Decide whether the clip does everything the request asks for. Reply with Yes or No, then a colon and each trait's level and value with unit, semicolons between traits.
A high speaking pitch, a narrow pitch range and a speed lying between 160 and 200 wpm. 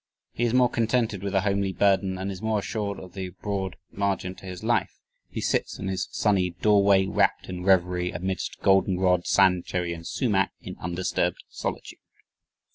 No: very low, 95 Hz; narrow, 1.8 semitones; average, 170 wpm